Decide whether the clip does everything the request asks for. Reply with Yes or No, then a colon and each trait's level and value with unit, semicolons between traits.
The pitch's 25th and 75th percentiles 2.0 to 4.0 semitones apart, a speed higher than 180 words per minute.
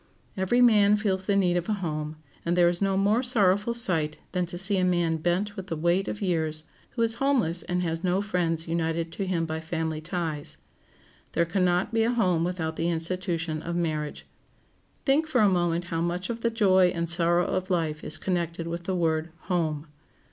Yes: average, 3.0 semitones; fast, 205 wpm